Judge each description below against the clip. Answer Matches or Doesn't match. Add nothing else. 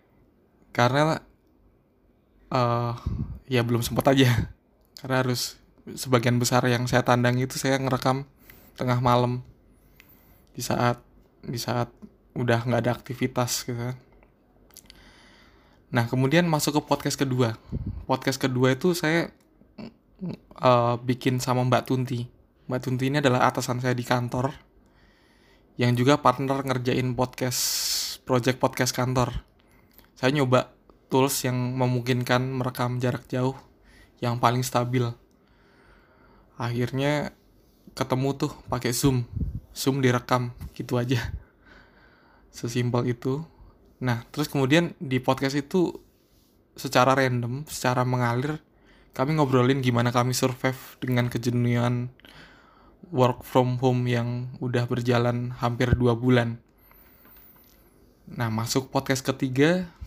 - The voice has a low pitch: Matches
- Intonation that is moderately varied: Doesn't match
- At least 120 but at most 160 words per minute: Doesn't match